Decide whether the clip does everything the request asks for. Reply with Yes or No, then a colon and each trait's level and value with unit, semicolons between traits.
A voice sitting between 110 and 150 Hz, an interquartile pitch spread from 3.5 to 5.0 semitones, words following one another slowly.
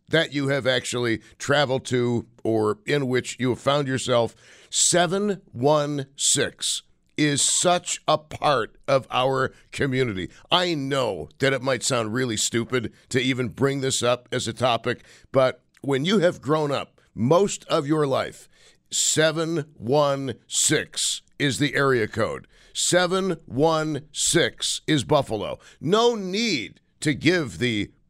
Yes: low, 135 Hz; average, 3.9 semitones; slow, 130 wpm